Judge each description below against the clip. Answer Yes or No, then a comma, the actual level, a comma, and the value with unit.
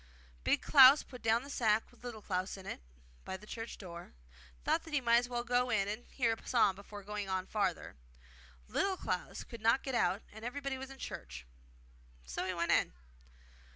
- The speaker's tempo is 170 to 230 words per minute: Yes, fast, 205 wpm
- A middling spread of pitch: Yes, average, 4.4 semitones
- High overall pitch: Yes, high, 225 Hz